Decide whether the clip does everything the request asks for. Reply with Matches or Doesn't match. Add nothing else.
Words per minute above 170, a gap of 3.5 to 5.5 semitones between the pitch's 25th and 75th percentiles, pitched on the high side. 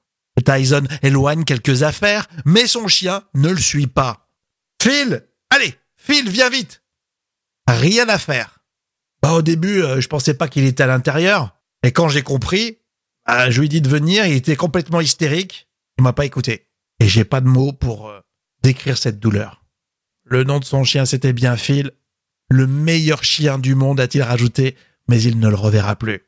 Doesn't match